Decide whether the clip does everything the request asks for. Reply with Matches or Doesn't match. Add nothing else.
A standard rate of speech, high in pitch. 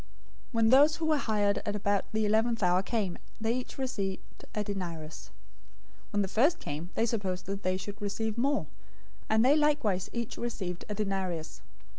Matches